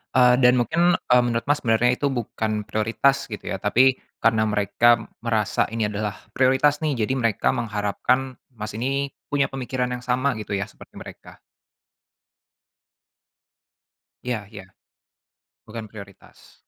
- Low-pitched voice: Yes, low, 120 Hz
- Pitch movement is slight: No, average, 3.3 semitones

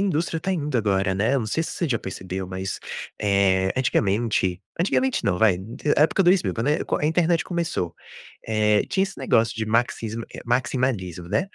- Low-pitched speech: Yes, low, 115 Hz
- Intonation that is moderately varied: No, wide, 8.6 semitones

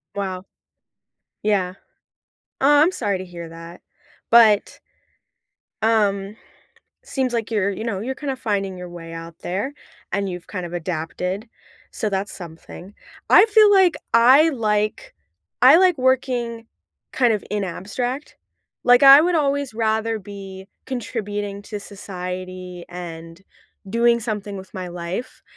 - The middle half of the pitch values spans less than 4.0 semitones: No, average, 4.8 semitones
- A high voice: Yes, high, 205 Hz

